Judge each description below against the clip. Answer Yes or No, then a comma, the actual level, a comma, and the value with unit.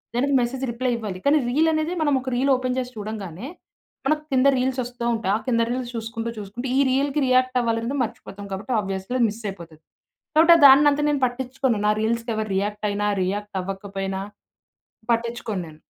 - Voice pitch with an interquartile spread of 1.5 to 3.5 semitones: No, average, 4.1 semitones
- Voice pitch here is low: No, high, 235 Hz